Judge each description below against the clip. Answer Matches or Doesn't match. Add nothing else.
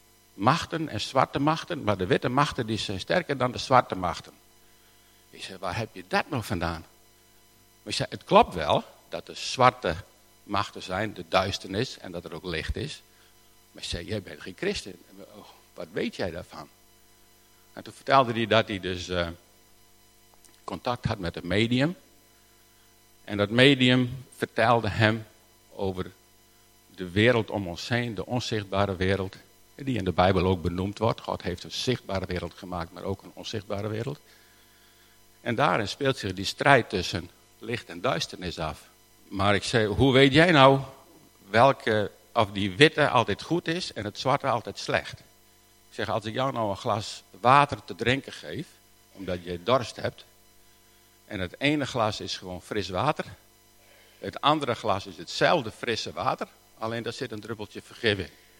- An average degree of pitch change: Matches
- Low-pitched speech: Matches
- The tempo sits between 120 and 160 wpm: Doesn't match